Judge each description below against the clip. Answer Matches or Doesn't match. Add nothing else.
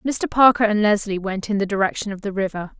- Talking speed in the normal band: Doesn't match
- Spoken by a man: Doesn't match